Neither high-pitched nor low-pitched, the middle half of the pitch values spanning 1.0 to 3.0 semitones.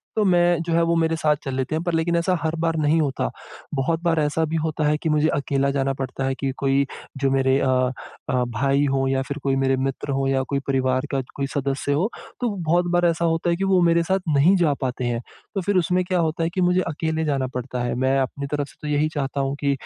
No: medium, 145 Hz; average, 3.7 semitones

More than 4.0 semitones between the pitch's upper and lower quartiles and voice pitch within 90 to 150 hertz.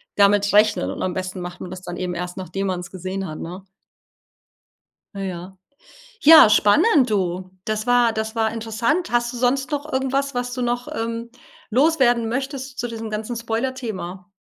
No: average, 4.7 semitones; high, 225 Hz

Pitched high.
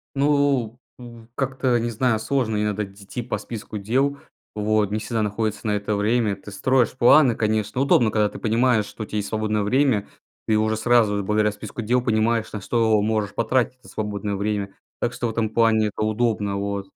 No: low, 110 Hz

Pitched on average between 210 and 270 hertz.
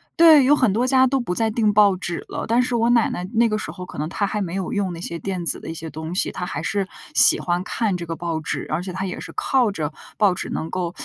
No: high, 195 Hz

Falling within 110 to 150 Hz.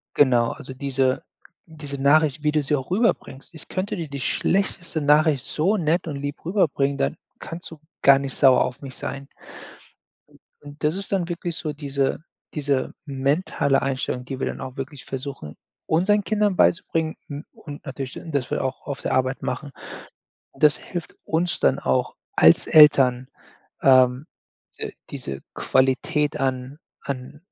Yes: medium, 140 Hz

